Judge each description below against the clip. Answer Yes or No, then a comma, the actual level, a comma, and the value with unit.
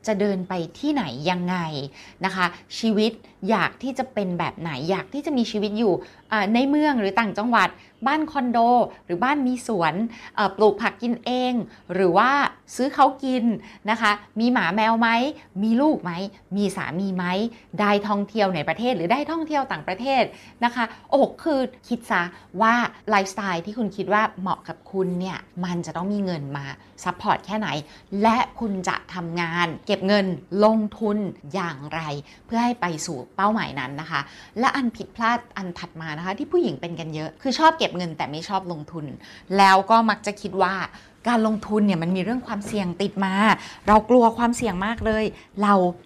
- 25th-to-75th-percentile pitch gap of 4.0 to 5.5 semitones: Yes, average, 4.4 semitones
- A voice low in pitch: No, high, 205 Hz